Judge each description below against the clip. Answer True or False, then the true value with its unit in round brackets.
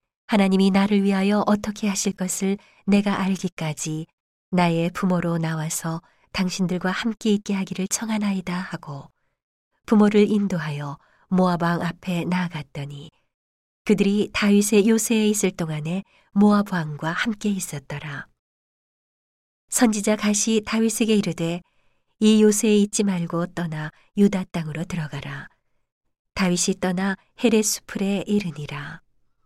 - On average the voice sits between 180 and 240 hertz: True (190 Hz)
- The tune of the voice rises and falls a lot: False (3.7 semitones)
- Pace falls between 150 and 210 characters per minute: False (275 characters per minute)